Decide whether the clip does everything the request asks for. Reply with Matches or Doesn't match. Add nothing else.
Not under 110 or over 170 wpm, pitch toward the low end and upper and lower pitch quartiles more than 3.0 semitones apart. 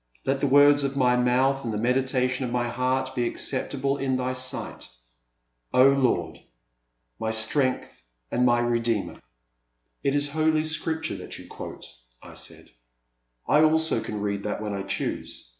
Matches